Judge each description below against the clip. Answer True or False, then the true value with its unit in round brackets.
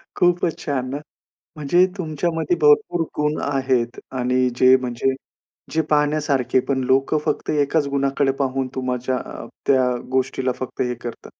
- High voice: False (135 Hz)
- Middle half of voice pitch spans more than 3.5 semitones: False (2.9 semitones)